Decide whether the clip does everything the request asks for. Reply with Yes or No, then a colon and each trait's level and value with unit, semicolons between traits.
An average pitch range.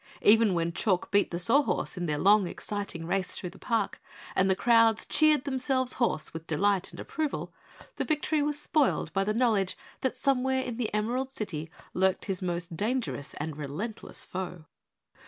No: wide, 6.1 semitones